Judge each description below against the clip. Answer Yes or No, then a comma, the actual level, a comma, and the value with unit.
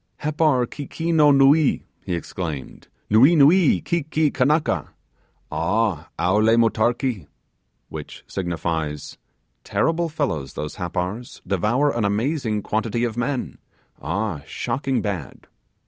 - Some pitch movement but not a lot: No, wide, 7.7 semitones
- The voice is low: Yes, low, 115 Hz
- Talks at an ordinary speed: No, slow, 105 wpm